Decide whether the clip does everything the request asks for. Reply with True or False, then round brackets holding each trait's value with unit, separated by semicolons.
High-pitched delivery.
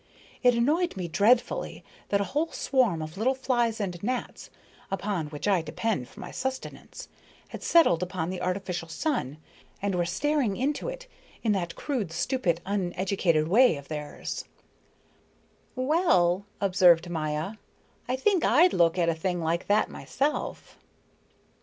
True (195 Hz)